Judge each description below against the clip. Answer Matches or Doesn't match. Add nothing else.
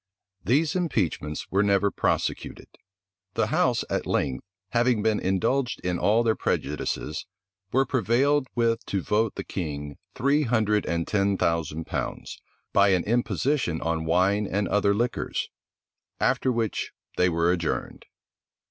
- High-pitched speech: Doesn't match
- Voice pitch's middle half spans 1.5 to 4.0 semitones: Doesn't match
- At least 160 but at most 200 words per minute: Doesn't match